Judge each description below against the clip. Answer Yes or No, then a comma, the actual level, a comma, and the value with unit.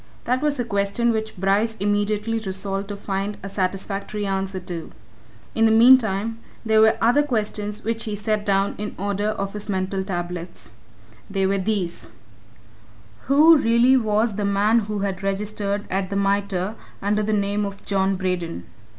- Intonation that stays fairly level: Yes, narrow, 2.0 semitones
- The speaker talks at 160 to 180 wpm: Yes, average, 165 wpm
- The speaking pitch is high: Yes, high, 205 Hz